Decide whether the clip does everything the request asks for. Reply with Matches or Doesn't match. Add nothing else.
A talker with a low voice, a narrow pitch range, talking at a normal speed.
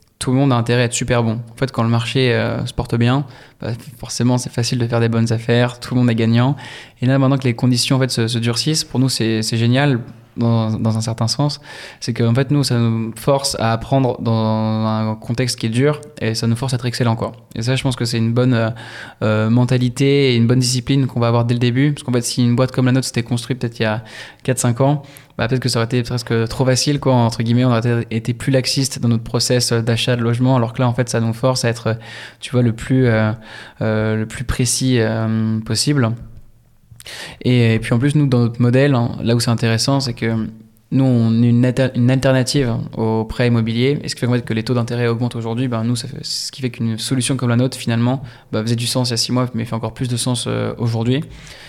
Doesn't match